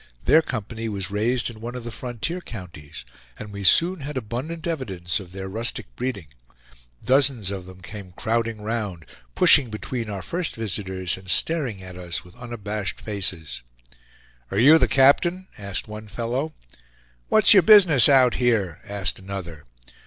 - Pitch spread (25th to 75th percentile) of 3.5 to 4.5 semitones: No, average, 5.2 semitones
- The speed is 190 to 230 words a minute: No, average, 155 wpm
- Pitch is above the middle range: No, low, 110 Hz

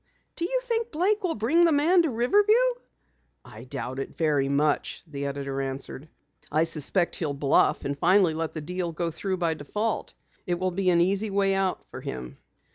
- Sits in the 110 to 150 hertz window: No, medium, 175 Hz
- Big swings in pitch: Yes, wide, 8.0 semitones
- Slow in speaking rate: No, average, 185 wpm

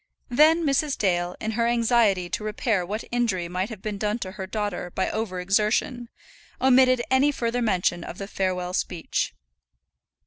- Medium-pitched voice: No, high, 215 Hz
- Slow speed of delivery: No, average, 165 wpm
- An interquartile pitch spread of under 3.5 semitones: No, average, 4.4 semitones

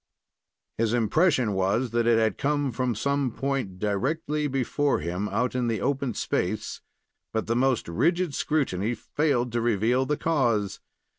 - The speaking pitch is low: Yes, low, 125 Hz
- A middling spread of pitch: Yes, average, 4.2 semitones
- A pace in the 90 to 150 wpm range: Yes, average, 145 wpm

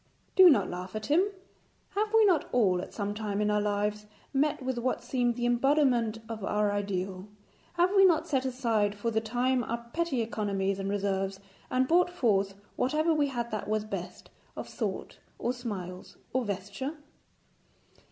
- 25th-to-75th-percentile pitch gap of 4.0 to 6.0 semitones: Yes, average, 4.6 semitones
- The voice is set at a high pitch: Yes, high, 230 Hz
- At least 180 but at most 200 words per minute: No, average, 170 wpm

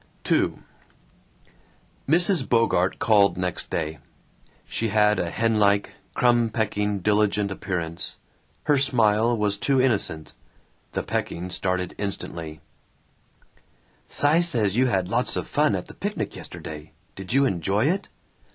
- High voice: No, low, 105 Hz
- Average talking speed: No, slow, 125 wpm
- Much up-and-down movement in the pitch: No, average, 4.5 semitones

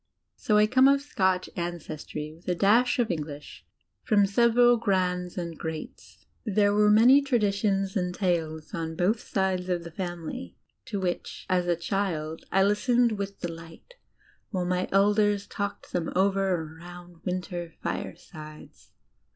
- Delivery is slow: No, average, 145 wpm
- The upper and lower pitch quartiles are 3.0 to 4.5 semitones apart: Yes, average, 3.3 semitones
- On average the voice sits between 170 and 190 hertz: Yes, medium, 185 Hz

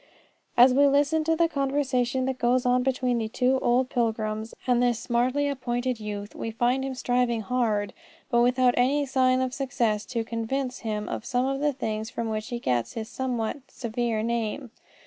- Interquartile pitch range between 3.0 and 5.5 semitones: No, narrow, 2.5 semitones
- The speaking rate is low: No, average, 185 wpm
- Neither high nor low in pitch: No, high, 245 Hz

